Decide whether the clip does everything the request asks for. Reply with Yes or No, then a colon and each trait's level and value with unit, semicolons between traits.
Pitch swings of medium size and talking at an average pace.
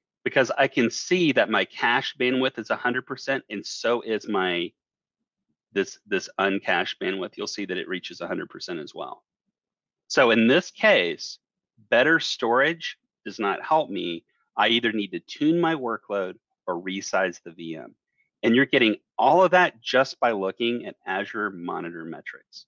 No: wide, 5.8 semitones; average, 160 wpm